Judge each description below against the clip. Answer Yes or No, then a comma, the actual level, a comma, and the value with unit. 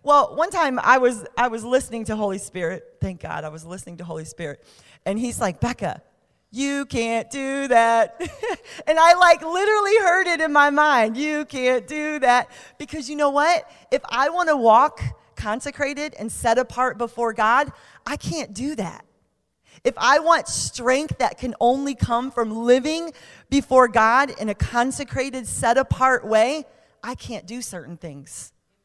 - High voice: Yes, very high, 255 Hz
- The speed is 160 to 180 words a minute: Yes, average, 170 wpm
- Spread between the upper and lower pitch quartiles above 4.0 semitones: Yes, average, 4.8 semitones